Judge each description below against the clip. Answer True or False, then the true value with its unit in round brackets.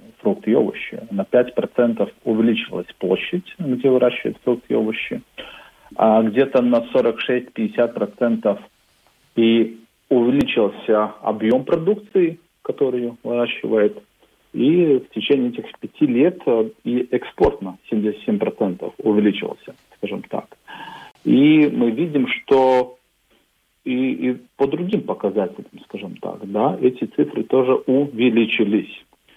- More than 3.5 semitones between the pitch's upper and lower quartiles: False (2.9 semitones)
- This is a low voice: True (120 Hz)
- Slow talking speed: True (105 wpm)